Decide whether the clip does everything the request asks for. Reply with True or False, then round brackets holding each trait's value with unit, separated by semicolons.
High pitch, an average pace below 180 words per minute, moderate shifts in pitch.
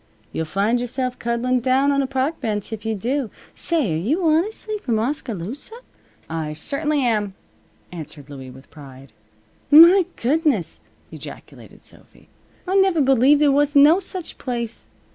False (255 Hz; 145 wpm; 6.3 semitones)